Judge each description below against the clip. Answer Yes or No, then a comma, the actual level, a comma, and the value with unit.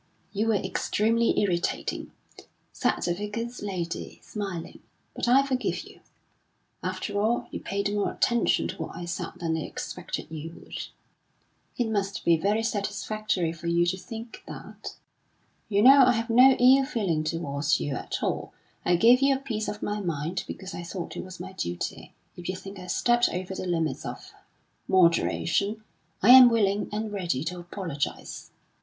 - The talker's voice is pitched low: No, high, 200 Hz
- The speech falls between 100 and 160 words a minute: No, average, 170 wpm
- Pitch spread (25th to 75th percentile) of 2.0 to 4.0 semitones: No, average, 4.6 semitones